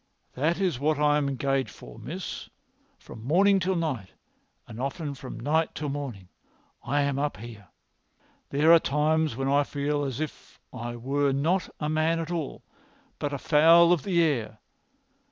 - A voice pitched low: No, medium, 145 Hz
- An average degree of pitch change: Yes, average, 3.1 semitones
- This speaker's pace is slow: No, average, 170 wpm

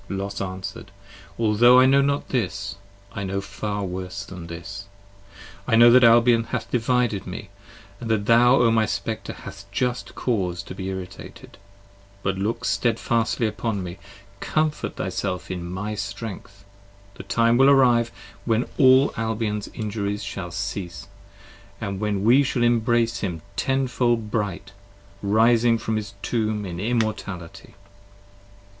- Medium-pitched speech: No, low, 110 Hz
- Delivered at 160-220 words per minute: No, average, 140 wpm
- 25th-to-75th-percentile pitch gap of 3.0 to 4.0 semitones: Yes, average, 3.3 semitones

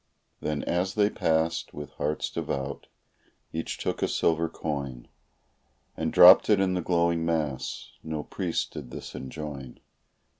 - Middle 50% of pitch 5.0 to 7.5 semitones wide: No, average, 2.9 semitones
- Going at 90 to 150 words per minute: Yes, average, 140 wpm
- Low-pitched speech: Yes, very low, 80 Hz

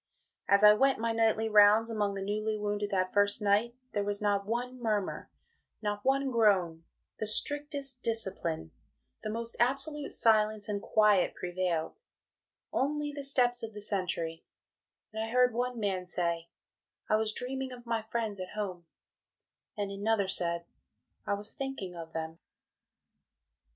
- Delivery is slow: No, average, 150 wpm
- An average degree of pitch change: Yes, average, 3.1 semitones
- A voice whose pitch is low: No, high, 210 Hz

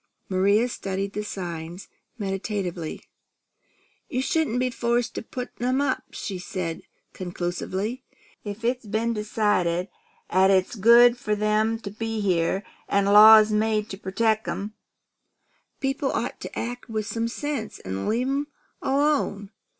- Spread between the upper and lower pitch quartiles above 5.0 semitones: No, average, 3.6 semitones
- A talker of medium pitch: No, high, 215 Hz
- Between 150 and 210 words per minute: No, slow, 135 wpm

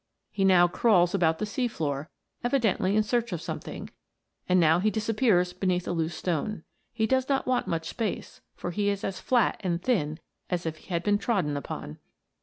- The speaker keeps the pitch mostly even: No, average, 4.4 semitones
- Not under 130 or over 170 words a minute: No, average, 190 wpm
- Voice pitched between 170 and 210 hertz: Yes, medium, 185 Hz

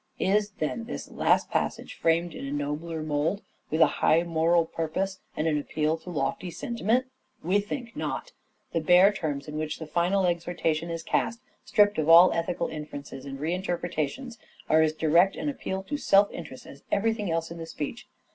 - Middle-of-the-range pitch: Yes, medium, 170 Hz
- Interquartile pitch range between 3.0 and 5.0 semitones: Yes, average, 3.9 semitones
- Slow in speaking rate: No, average, 180 wpm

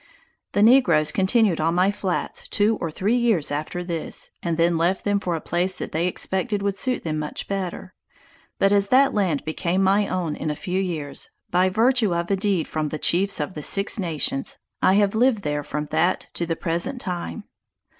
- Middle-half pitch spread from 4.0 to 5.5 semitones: No, average, 3.5 semitones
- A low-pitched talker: No, medium, 185 Hz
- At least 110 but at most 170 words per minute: No, average, 200 wpm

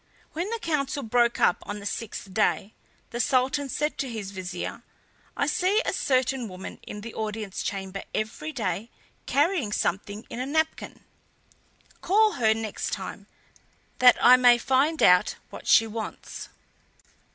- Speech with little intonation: No, average, 5.3 semitones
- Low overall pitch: No, high, 240 Hz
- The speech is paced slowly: No, average, 150 wpm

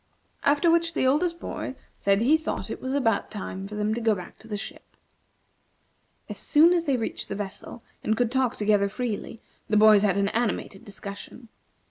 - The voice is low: No, high, 225 Hz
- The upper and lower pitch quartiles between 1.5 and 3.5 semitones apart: No, average, 4.5 semitones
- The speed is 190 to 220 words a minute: Yes, average, 195 wpm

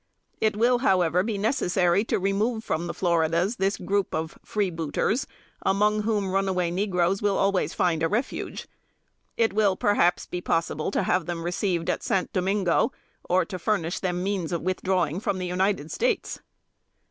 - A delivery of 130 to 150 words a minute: No, average, 160 wpm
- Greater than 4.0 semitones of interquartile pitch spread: No, average, 2.8 semitones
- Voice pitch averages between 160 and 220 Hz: Yes, high, 190 Hz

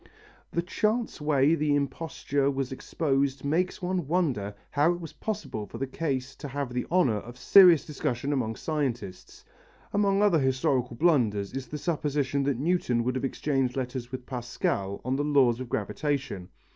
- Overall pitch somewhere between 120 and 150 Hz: Yes, medium, 140 Hz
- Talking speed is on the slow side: No, average, 165 wpm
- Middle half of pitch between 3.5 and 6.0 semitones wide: Yes, average, 3.9 semitones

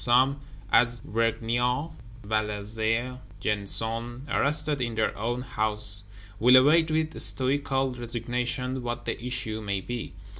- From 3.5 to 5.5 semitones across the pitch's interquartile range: No, average, 2.8 semitones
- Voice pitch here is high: No, low, 120 Hz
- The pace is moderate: No, slow, 115 wpm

